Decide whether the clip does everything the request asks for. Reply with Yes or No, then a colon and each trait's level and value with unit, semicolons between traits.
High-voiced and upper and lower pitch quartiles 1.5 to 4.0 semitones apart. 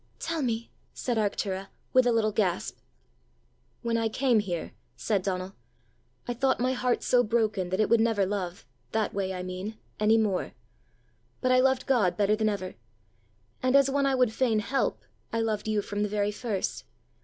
Yes: high, 220 Hz; average, 3.6 semitones